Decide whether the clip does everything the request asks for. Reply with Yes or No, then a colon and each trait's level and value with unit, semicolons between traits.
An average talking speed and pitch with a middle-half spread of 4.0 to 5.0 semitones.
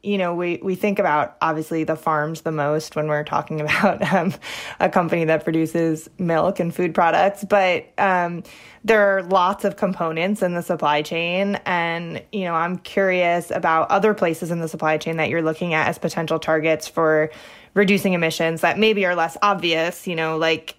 No: average, 190 wpm; average, 2.9 semitones